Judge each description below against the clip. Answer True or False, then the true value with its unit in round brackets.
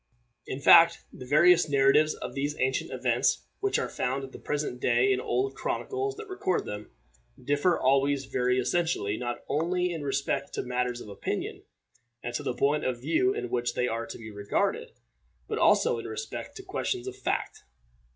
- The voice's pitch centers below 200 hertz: True (140 Hz)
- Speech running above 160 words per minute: True (185 wpm)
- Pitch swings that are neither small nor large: False (5.8 semitones)